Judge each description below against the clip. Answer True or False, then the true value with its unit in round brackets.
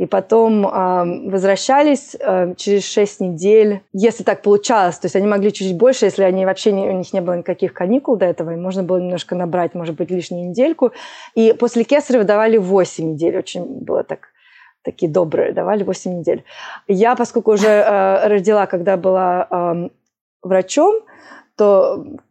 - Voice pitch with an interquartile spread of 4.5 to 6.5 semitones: False (3.5 semitones)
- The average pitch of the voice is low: False (195 Hz)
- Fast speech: True (165 wpm)